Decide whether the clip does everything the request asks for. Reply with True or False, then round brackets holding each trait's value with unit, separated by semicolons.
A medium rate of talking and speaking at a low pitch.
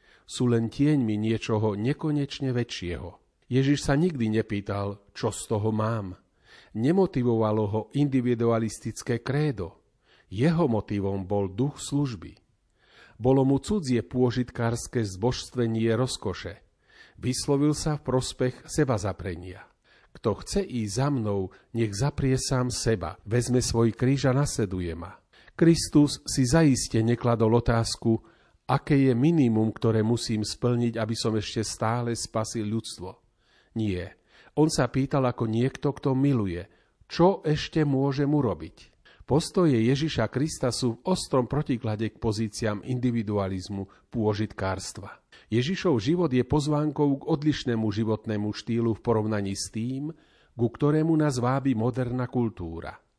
True (120 wpm; 120 Hz)